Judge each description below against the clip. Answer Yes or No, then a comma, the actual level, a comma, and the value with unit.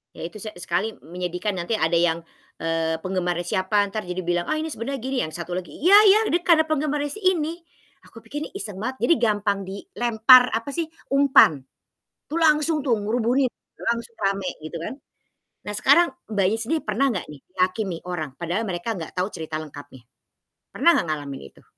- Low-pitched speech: No, high, 215 Hz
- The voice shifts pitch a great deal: Yes, wide, 7.8 semitones